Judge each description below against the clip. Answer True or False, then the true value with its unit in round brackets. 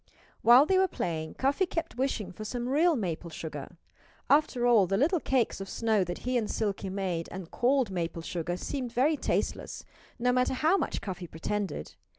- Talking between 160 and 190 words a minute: True (180 wpm)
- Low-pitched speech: False (225 Hz)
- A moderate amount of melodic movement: False (6.6 semitones)